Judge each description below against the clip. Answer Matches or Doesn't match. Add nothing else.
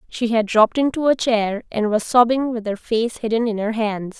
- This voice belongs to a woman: Matches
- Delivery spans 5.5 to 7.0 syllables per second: Doesn't match